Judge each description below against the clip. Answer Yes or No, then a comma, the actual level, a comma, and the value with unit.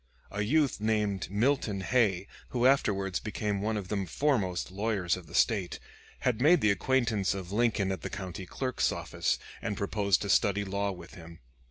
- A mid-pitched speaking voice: No, low, 100 Hz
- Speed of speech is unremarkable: Yes, average, 175 wpm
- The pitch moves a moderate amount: Yes, average, 3.1 semitones